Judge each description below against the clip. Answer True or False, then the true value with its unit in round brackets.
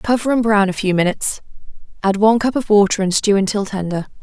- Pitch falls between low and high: False (205 Hz)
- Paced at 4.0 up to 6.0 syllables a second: False (6.3 syllables/s)